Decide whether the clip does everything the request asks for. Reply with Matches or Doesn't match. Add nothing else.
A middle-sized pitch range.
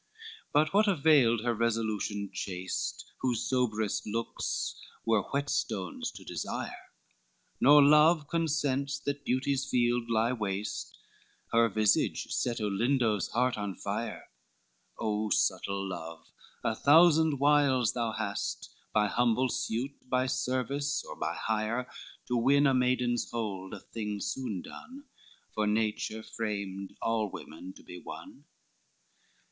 Matches